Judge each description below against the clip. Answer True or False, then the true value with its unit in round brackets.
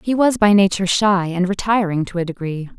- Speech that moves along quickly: True (215 wpm)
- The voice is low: False (190 Hz)